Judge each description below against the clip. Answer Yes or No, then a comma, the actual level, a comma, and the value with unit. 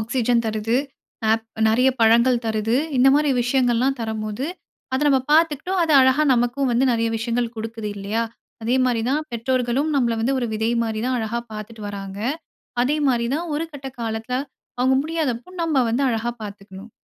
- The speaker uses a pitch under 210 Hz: No, high, 235 Hz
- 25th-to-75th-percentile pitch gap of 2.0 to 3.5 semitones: Yes, average, 3.0 semitones